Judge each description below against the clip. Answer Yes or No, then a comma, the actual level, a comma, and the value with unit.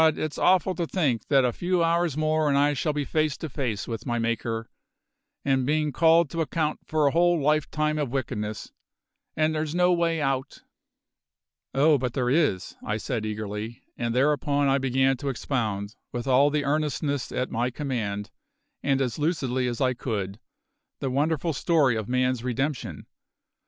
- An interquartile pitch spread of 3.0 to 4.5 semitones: Yes, average, 4.2 semitones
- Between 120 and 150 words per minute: No, average, 170 wpm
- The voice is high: No, low, 135 Hz